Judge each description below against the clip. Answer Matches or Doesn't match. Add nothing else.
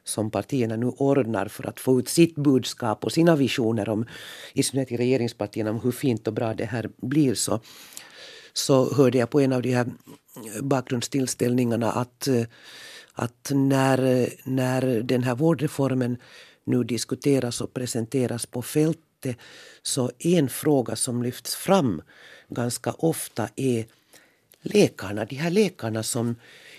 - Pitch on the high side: Doesn't match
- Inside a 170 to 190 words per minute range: Doesn't match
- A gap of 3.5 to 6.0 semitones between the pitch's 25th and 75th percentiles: Doesn't match